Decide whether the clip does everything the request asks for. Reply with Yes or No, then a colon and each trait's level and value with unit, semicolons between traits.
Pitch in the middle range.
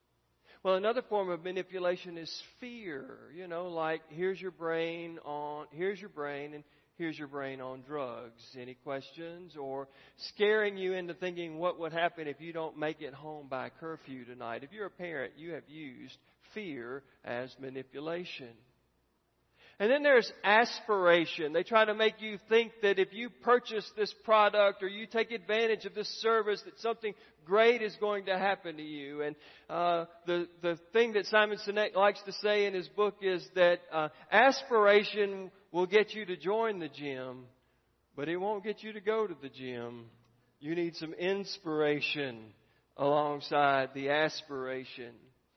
Yes: medium, 170 Hz